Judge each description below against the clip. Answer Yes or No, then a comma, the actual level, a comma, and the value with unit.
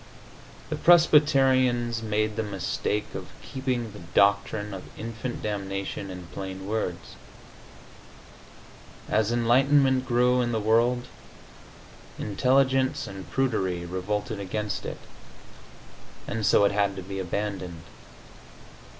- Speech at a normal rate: No, slow, 105 wpm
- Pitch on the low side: Yes, low, 110 Hz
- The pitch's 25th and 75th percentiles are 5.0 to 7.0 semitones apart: No, average, 4.2 semitones